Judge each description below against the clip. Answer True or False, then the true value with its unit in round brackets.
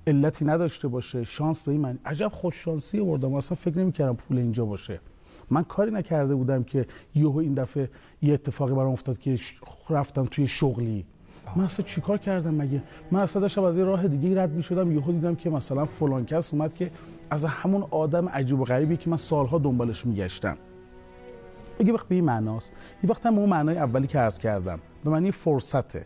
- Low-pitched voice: False (150 Hz)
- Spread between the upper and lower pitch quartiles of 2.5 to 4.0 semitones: False (5.1 semitones)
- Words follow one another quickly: True (185 wpm)